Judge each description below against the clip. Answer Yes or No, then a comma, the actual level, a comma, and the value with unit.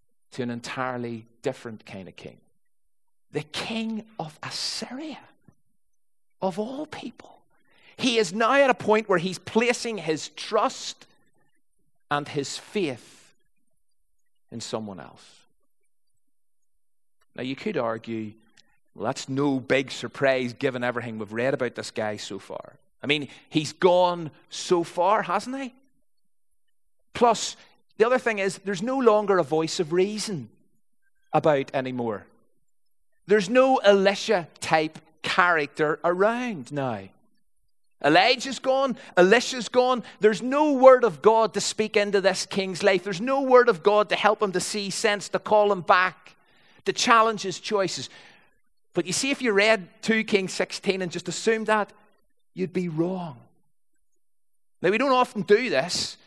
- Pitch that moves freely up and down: Yes, wide, 6.8 semitones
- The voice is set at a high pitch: Yes, high, 200 Hz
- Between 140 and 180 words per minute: Yes, average, 145 wpm